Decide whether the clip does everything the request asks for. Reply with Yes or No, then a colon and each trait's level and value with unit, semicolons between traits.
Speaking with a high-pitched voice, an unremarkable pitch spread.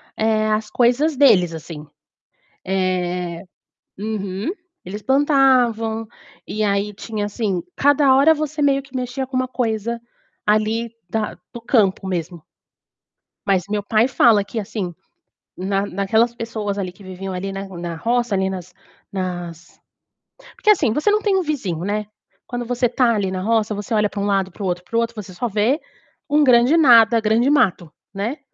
Yes: high, 215 Hz; average, 4.2 semitones